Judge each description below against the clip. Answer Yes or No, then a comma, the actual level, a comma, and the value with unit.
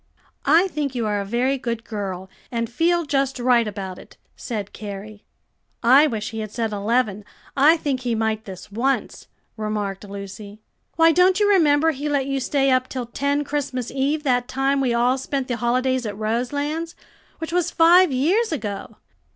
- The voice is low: No, very high, 255 Hz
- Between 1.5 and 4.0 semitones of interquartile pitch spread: No, average, 5.0 semitones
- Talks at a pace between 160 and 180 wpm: Yes, average, 175 wpm